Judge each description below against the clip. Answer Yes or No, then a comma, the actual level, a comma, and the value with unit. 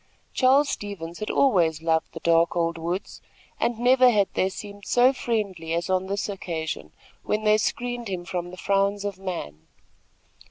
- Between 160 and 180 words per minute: Yes, average, 165 wpm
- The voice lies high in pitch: Yes, high, 195 Hz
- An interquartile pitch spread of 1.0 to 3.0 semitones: No, average, 4.1 semitones